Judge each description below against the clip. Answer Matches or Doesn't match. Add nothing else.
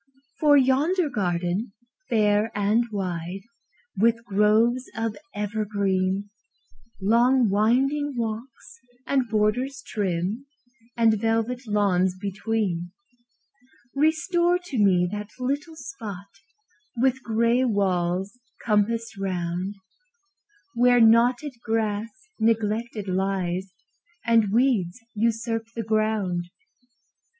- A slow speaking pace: Matches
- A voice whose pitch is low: Doesn't match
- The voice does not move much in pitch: Doesn't match